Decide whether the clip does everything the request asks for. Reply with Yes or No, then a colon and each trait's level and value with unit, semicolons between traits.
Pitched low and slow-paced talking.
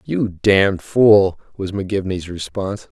Yes: very low, 95 Hz; slow, 120 wpm